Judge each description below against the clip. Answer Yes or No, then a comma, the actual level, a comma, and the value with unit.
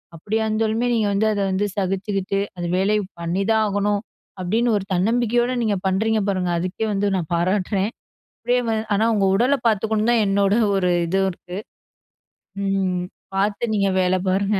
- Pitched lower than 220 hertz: Yes, high, 200 Hz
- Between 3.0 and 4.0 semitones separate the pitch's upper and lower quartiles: No, narrow, 2.6 semitones